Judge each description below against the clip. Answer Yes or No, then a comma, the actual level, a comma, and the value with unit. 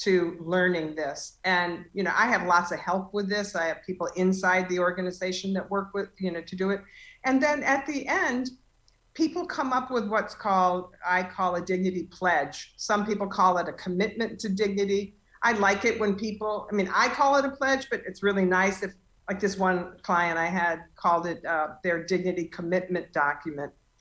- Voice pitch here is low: No, medium, 185 Hz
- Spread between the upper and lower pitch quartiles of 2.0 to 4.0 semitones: Yes, average, 2.9 semitones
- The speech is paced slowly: No, average, 200 wpm